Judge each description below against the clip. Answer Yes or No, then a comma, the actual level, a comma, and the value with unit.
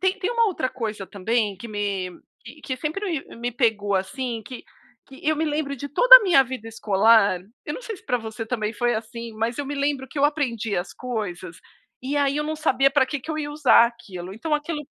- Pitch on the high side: Yes, very high, 250 Hz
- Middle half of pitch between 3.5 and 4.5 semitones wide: No, average, 5.1 semitones